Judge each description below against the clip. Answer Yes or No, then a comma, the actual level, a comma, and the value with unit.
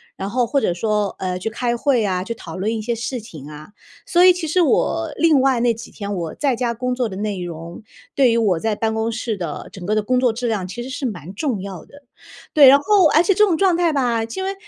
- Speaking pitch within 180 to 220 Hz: No, high, 230 Hz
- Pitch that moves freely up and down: Yes, wide, 5.7 semitones